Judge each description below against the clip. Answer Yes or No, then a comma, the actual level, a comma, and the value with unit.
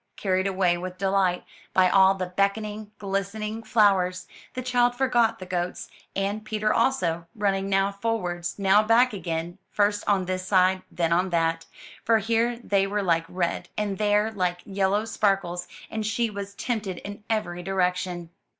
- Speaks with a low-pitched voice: No, high, 195 Hz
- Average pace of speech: Yes, average, 160 wpm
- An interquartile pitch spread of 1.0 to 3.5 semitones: Yes, average, 2.8 semitones